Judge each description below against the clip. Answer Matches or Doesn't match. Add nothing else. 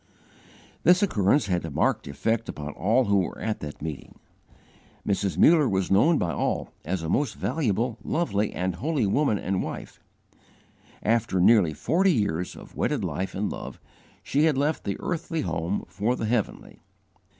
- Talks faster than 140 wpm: Matches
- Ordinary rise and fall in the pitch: Doesn't match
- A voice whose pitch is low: Matches